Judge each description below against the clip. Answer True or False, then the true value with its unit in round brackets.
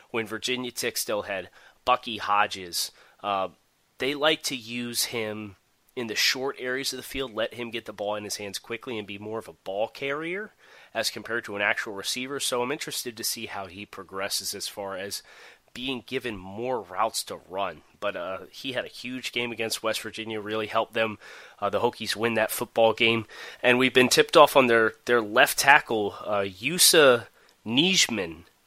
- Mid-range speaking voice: False (115 Hz)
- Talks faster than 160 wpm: True (195 wpm)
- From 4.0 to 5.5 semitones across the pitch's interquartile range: False (3.0 semitones)